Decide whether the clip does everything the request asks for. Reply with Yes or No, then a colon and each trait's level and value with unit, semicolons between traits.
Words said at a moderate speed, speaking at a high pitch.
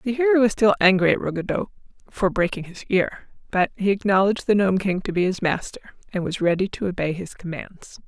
No: fast, 210 wpm; high, 195 Hz